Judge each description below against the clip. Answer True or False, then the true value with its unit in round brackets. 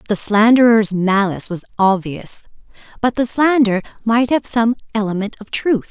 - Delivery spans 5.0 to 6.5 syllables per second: False (4.8 syllables/s)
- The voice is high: True (220 Hz)